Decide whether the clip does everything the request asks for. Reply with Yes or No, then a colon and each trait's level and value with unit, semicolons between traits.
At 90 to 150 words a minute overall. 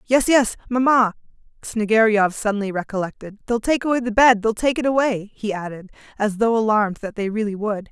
No: average, 180 wpm